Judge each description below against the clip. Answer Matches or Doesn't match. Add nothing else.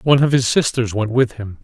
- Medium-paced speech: Doesn't match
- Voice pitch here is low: Matches